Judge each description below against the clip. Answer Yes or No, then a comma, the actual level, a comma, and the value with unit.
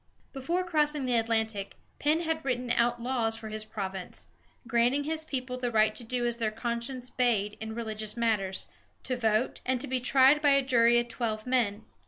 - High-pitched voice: Yes, high, 240 Hz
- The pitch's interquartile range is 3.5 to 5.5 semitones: No, average, 2.9 semitones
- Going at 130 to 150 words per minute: No, average, 190 wpm